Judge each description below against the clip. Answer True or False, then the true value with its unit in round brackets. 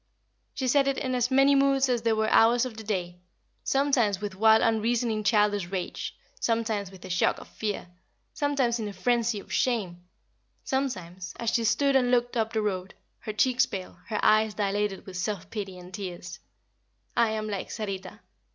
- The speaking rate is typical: True (180 wpm)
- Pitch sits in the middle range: False (220 Hz)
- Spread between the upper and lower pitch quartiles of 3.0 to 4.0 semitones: True (3.7 semitones)